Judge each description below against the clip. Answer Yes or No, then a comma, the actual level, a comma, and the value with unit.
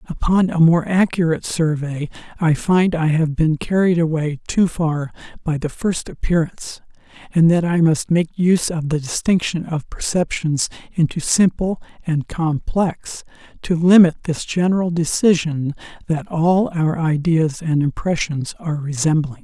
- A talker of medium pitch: Yes, medium, 165 Hz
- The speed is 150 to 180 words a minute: No, average, 140 wpm